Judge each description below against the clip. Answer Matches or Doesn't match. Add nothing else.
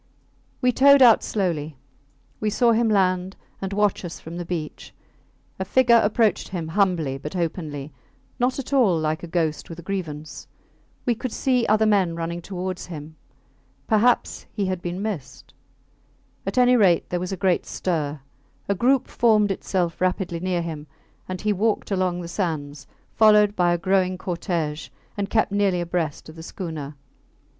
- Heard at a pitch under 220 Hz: Matches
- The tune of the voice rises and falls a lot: Doesn't match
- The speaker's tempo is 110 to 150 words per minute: Doesn't match